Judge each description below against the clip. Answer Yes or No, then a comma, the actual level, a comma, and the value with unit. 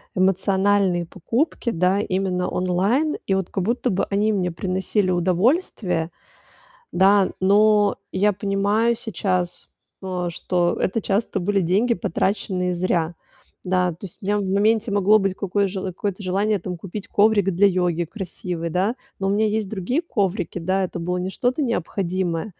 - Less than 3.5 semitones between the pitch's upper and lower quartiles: Yes, narrow, 2.4 semitones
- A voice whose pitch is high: Yes, high, 195 Hz